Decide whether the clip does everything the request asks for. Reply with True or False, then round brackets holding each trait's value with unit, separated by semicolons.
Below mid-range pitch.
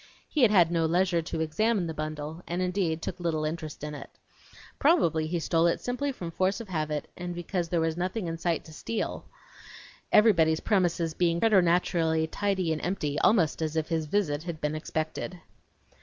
False (170 Hz)